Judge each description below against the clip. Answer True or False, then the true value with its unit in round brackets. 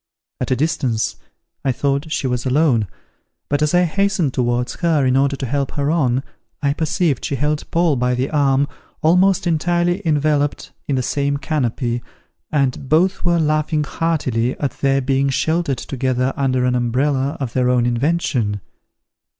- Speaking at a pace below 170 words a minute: True (160 wpm)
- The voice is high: False (140 Hz)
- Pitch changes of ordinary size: True (3.6 semitones)